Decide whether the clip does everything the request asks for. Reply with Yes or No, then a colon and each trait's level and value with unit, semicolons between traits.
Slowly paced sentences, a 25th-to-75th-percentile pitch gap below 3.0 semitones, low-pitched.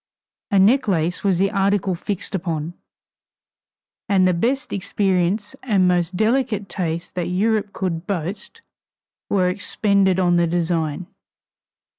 No: slow, 120 wpm; narrow, 2.6 semitones; high, 190 Hz